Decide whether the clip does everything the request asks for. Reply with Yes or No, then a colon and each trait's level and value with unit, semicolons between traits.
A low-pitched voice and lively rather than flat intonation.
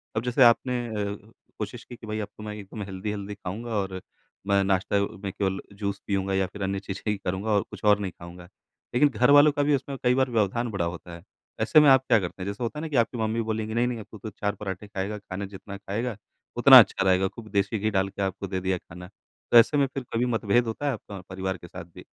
No: low, 105 Hz; average, 3.3 semitones